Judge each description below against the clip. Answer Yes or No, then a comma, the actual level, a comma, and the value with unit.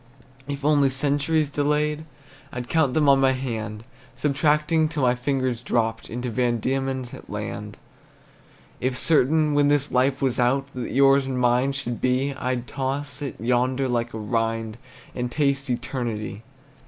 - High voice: No, low, 130 Hz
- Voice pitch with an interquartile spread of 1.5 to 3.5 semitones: Yes, average, 2.7 semitones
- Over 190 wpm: No, average, 150 wpm